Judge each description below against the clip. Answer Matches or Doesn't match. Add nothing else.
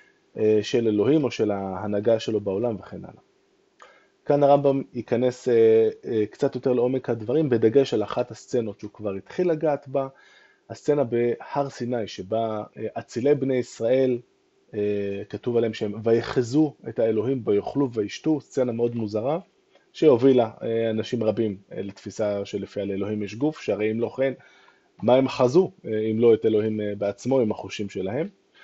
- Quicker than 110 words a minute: Matches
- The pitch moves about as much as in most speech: Matches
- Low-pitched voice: Matches